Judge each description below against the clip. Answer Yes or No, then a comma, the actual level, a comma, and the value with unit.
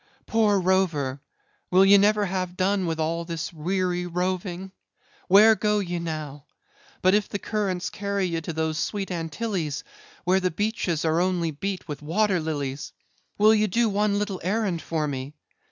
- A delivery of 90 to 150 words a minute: No, average, 165 wpm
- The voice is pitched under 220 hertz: Yes, medium, 185 Hz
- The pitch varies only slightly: No, average, 3.7 semitones